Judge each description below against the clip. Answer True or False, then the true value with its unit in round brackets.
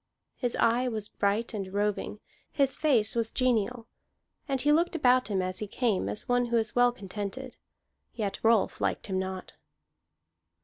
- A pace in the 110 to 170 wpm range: True (165 wpm)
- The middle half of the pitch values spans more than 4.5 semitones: False (3.6 semitones)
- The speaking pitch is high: True (225 Hz)